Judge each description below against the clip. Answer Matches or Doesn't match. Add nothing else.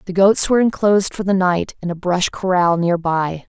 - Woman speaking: Matches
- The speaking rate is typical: Doesn't match